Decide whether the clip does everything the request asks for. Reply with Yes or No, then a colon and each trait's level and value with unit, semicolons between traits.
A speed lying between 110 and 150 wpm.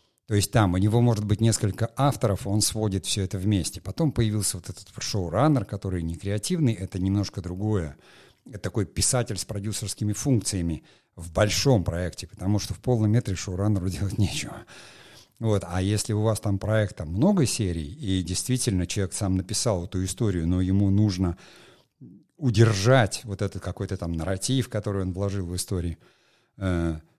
No: fast, 160 wpm